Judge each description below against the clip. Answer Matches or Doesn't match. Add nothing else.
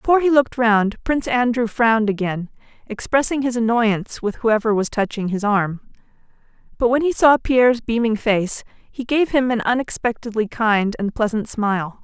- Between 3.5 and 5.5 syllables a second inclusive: Matches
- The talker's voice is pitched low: Doesn't match